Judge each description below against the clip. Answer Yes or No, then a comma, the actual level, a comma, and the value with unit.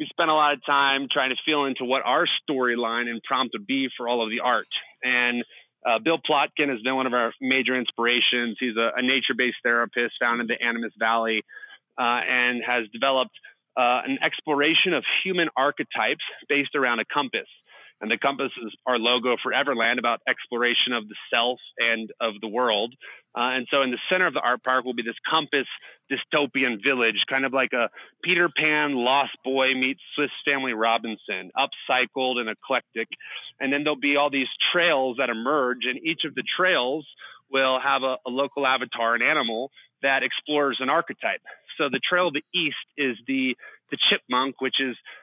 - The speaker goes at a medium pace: Yes, average, 190 wpm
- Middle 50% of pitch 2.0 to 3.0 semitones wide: Yes, average, 2.7 semitones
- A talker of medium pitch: No, low, 130 Hz